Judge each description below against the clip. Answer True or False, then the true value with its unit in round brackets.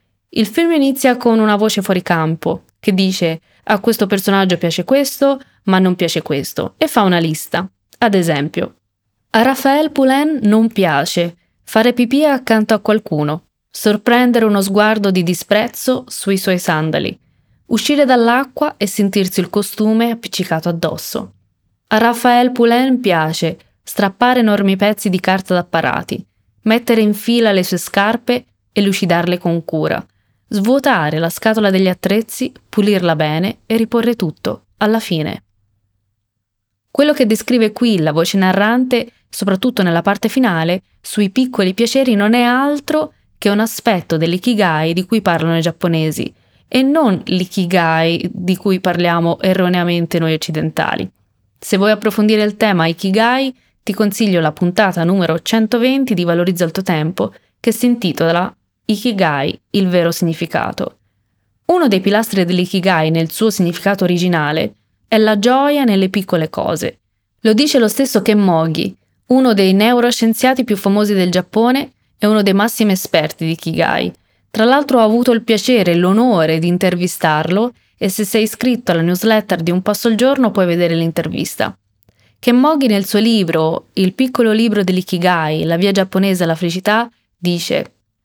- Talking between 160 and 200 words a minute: False (145 wpm)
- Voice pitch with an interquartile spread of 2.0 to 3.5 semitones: False (5.1 semitones)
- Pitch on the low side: False (200 Hz)